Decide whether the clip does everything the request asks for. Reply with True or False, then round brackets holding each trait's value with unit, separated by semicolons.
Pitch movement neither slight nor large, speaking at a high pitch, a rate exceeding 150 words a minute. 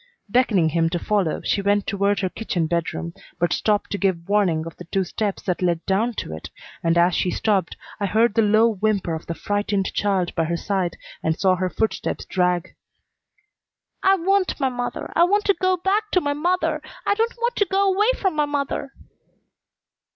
False (8.6 semitones; 205 Hz; 195 wpm)